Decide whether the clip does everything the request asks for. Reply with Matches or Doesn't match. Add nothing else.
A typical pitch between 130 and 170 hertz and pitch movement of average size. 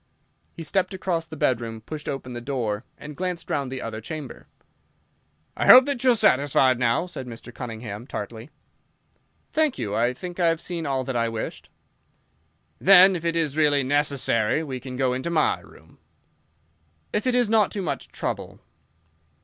Doesn't match